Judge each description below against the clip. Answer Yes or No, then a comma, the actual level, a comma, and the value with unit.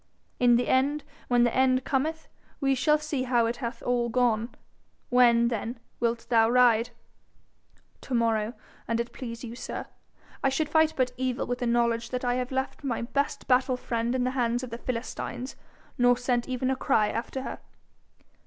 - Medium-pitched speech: No, high, 245 Hz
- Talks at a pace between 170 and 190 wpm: Yes, average, 180 wpm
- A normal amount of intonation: No, narrow, 1.8 semitones